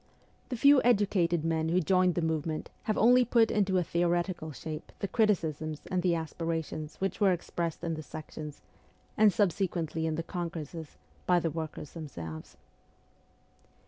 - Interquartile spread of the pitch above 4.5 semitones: No, average, 3.1 semitones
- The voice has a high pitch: No, medium, 170 Hz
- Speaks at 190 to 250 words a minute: No, average, 150 wpm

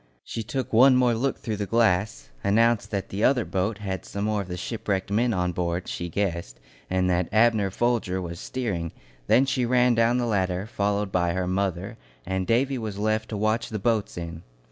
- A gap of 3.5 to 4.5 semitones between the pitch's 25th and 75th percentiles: Yes, average, 3.8 semitones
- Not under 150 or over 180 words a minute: No, average, 200 wpm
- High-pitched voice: No, low, 105 Hz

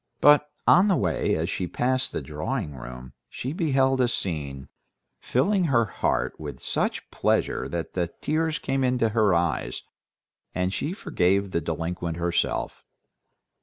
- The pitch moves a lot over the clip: Yes, wide, 8.0 semitones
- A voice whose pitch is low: Yes, low, 100 Hz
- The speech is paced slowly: No, average, 145 wpm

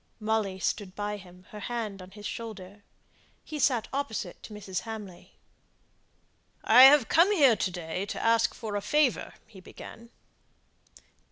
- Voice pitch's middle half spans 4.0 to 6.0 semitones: No, average, 3.4 semitones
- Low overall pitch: No, high, 215 Hz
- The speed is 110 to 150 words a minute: Yes, average, 140 wpm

